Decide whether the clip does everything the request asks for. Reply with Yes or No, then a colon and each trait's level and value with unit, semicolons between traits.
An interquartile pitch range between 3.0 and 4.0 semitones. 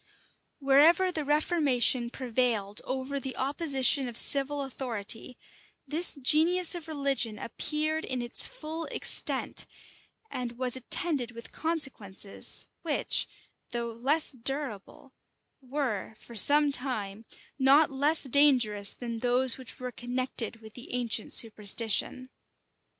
Yes: average, 3.7 semitones